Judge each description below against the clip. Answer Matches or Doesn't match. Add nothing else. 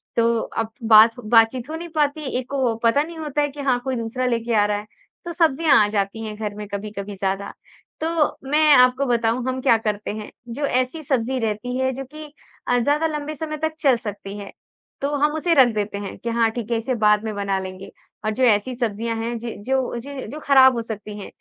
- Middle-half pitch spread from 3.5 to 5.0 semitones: Matches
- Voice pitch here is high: Matches